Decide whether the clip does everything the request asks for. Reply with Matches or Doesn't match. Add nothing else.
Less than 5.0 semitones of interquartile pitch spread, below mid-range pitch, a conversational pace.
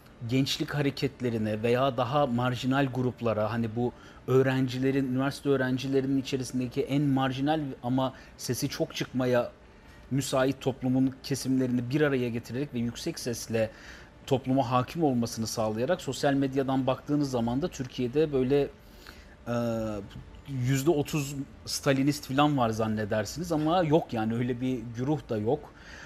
Matches